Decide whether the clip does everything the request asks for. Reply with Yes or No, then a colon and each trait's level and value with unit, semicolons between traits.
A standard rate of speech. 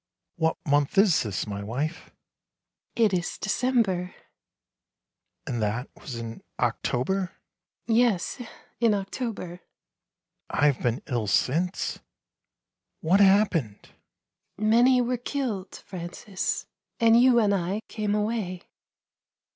No: slow, 125 wpm